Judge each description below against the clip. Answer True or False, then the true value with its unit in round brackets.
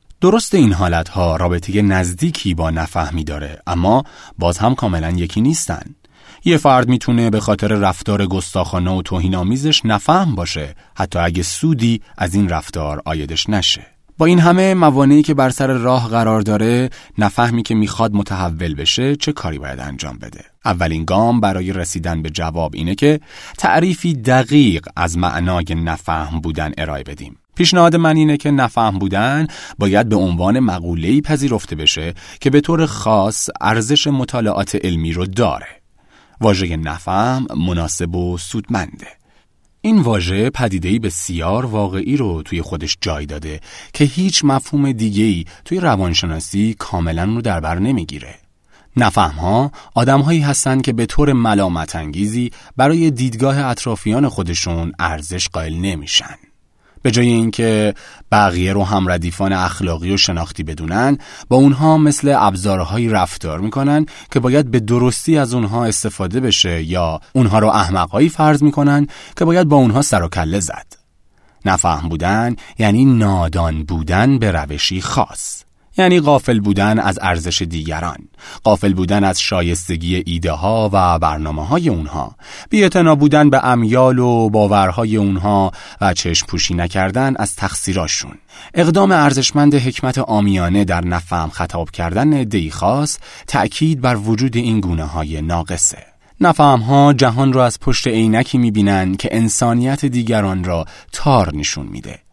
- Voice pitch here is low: True (105 Hz)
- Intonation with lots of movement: True (6.8 semitones)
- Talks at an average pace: True (140 wpm)